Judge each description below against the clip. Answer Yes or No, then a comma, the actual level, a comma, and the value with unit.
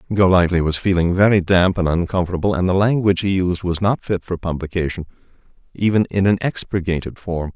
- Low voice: Yes, very low, 90 Hz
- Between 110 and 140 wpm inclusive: No, average, 175 wpm